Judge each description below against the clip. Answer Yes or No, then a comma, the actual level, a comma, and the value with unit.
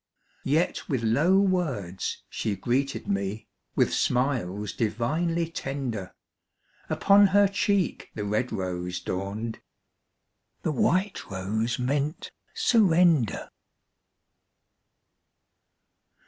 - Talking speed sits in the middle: No, slow, 85 wpm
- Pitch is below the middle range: Yes, low, 125 Hz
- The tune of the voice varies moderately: No, wide, 8.5 semitones